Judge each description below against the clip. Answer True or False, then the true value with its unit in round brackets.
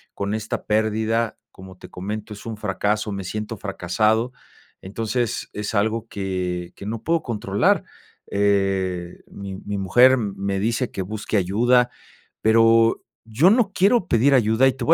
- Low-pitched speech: True (110 Hz)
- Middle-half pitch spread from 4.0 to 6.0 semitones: False (2.7 semitones)